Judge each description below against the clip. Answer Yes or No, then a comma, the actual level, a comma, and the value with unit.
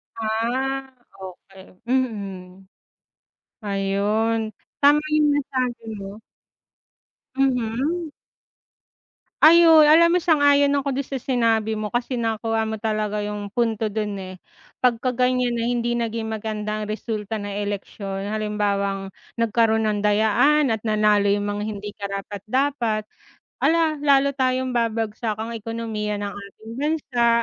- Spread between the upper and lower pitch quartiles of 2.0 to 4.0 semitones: Yes, average, 3.7 semitones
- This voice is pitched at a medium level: No, high, 225 Hz